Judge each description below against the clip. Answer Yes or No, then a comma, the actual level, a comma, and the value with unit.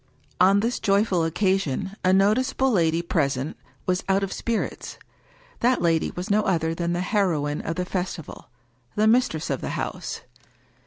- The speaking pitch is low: No, medium, 185 Hz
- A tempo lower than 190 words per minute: Yes, average, 160 wpm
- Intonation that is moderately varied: Yes, average, 3.7 semitones